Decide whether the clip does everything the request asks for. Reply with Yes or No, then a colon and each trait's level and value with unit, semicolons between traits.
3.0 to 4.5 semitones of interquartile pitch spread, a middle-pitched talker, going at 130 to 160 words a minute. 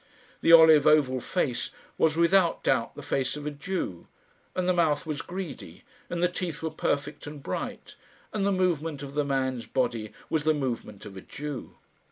No: average, 4.1 semitones; medium, 150 Hz; average, 185 wpm